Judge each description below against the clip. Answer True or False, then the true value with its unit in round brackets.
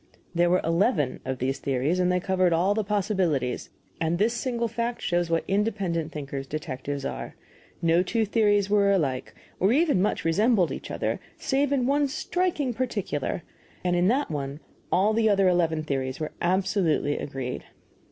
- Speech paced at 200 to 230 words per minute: False (165 wpm)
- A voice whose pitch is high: False (180 Hz)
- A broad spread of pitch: True (5.8 semitones)